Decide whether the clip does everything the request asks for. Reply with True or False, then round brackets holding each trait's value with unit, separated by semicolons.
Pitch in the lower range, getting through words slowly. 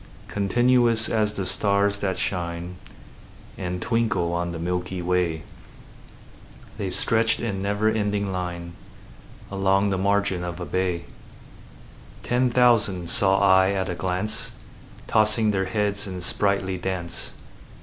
True (95 Hz; 125 wpm)